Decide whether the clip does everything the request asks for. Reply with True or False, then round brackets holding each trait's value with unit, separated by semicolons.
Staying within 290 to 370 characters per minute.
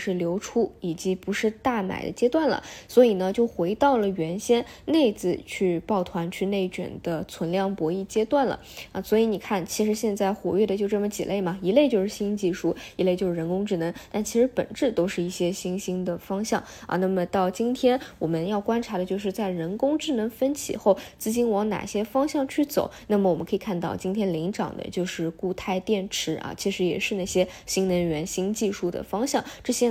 True (305 characters per minute)